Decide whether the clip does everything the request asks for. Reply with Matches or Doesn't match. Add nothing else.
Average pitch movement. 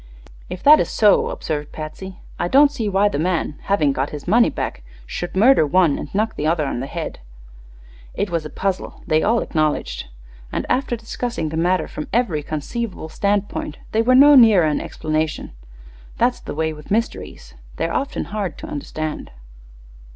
Doesn't match